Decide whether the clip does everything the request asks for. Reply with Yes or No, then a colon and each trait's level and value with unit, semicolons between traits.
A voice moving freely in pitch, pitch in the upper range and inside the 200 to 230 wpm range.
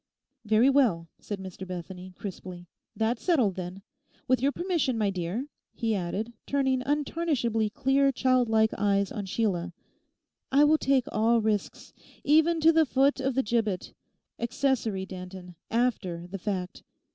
No: wide, 6.0 semitones; high, 225 Hz; slow, 135 wpm